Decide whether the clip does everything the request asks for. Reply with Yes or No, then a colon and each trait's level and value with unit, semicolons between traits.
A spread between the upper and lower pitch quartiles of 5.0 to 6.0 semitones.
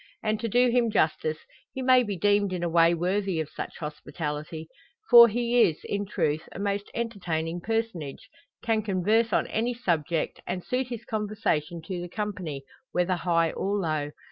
Yes: average, 5.3 semitones